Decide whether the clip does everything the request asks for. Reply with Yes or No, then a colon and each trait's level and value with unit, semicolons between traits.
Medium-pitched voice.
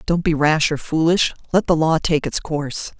Yes: medium, 155 Hz